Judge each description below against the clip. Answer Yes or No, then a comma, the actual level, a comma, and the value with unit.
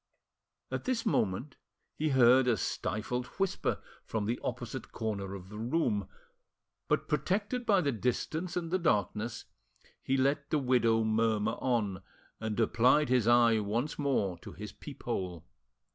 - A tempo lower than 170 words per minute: Yes, average, 145 wpm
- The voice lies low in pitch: Yes, low, 120 Hz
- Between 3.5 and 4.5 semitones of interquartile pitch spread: No, average, 4.9 semitones